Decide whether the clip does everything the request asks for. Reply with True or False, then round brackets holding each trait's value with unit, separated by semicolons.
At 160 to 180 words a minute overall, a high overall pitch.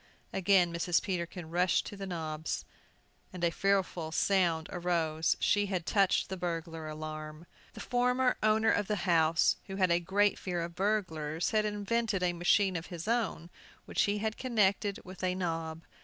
False (170 wpm; 180 Hz)